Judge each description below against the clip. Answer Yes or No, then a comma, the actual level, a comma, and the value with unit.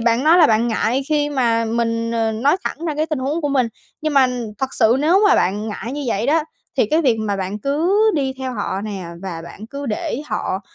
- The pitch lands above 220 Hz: Yes, very high, 250 Hz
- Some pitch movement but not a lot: Yes, average, 4.8 semitones